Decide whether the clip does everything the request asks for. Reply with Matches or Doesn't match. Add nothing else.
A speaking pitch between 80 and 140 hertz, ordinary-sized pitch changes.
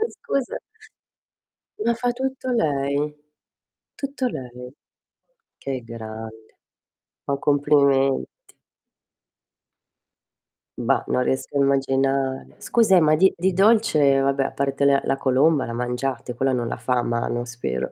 Matches